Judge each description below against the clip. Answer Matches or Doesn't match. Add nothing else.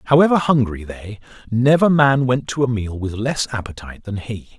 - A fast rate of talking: Doesn't match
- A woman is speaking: Doesn't match